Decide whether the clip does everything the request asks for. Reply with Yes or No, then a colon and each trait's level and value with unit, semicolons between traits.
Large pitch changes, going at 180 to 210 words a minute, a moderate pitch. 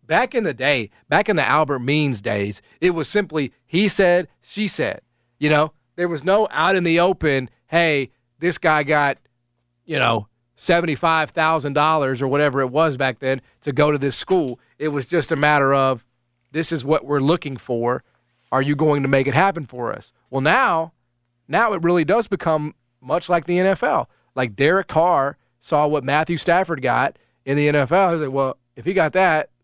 No: average, 4.3 semitones; average, 190 wpm; medium, 150 Hz